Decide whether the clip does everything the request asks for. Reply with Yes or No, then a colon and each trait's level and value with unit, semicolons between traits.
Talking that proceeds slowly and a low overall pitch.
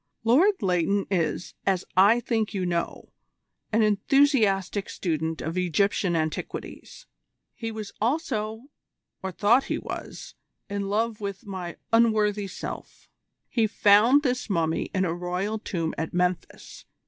No: slow, 130 wpm; high, 200 Hz